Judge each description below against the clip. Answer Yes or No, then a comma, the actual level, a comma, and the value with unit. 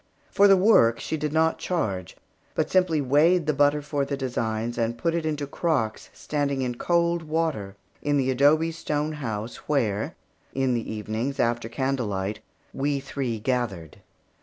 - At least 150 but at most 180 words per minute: Yes, average, 160 wpm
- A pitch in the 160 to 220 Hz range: No, medium, 140 Hz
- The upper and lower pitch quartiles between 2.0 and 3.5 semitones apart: No, average, 5.1 semitones